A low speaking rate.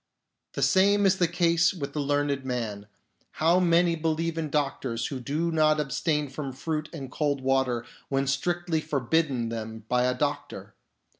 No: average, 160 wpm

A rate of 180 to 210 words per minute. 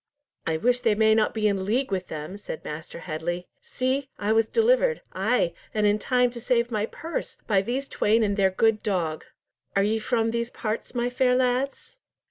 Yes: average, 190 wpm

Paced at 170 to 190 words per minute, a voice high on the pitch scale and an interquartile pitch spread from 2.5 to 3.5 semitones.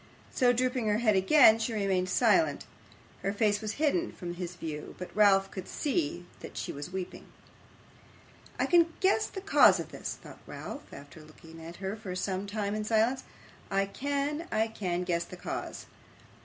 No: average, 175 wpm; high, 205 Hz; average, 5.3 semitones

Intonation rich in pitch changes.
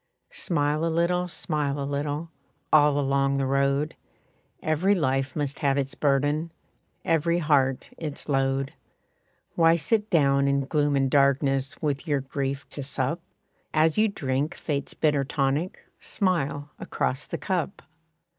No: average, 2.8 semitones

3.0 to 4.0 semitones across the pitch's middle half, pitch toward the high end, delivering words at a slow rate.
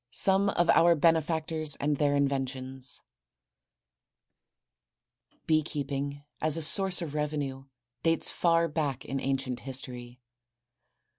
No: average, 3.3 semitones; medium, 145 Hz; slow, 105 wpm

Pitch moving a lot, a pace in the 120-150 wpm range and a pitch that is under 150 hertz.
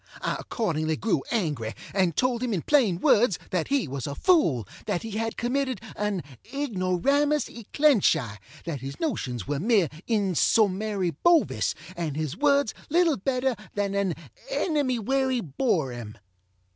No: wide, 8.5 semitones; average, 140 wpm; high, 205 Hz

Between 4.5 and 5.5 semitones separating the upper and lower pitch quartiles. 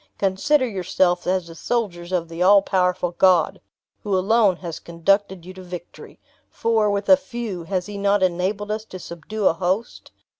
No: average, 2.7 semitones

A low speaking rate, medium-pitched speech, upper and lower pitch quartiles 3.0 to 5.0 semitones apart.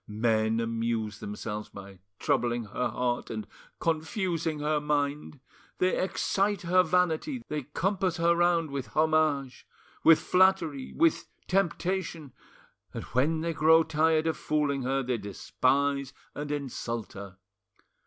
No: slow, 125 wpm; medium, 150 Hz; wide, 5.6 semitones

